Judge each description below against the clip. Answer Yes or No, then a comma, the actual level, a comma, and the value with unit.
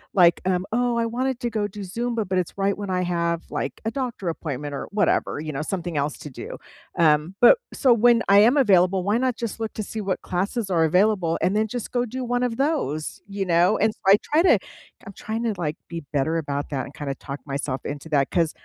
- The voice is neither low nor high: No, high, 195 Hz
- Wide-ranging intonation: Yes, wide, 5.8 semitones